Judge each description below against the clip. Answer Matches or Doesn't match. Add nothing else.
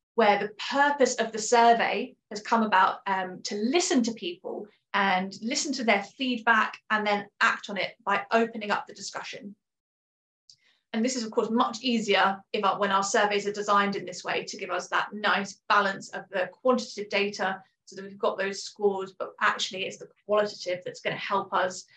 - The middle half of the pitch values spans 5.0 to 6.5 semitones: Doesn't match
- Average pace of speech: Matches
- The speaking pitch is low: Doesn't match